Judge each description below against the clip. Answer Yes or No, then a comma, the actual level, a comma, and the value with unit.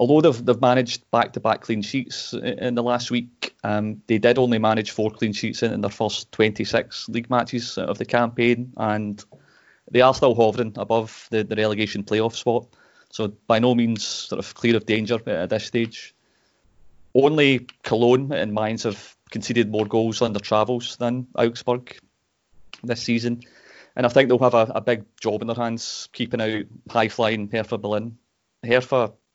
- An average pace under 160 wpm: No, average, 175 wpm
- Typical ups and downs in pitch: No, narrow, 2.0 semitones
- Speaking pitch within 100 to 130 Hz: Yes, low, 115 Hz